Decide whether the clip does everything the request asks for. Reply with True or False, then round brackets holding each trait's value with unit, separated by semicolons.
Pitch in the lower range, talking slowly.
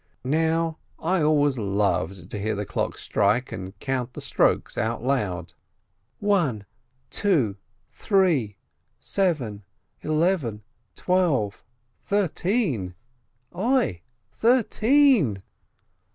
True (130 Hz; 115 wpm)